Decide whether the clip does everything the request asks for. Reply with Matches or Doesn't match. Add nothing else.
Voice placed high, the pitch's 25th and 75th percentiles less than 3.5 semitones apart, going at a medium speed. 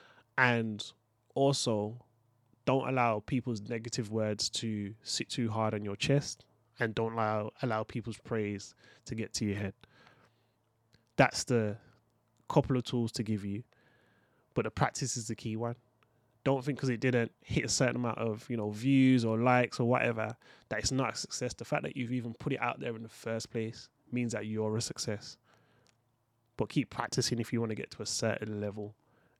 Doesn't match